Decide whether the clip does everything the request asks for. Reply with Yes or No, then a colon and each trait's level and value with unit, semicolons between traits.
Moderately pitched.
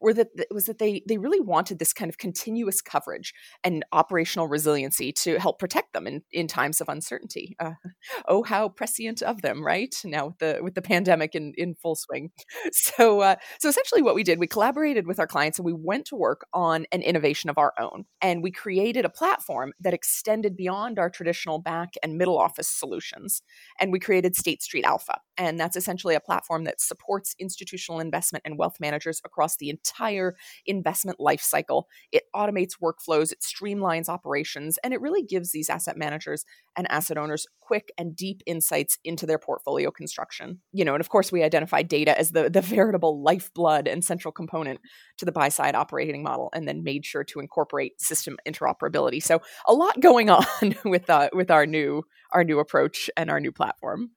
Yes: medium, 175 Hz